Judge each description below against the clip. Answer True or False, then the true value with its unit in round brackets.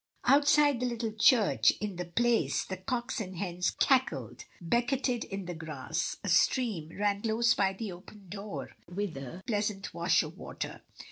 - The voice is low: False (210 Hz)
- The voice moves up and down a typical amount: True (4.4 semitones)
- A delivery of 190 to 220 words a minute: False (160 wpm)